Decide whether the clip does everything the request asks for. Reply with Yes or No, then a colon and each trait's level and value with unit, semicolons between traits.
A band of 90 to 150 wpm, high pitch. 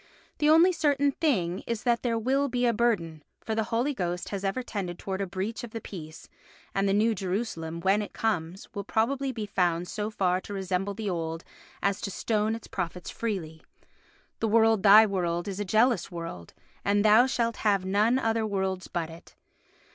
No: average, 195 wpm; high, 205 Hz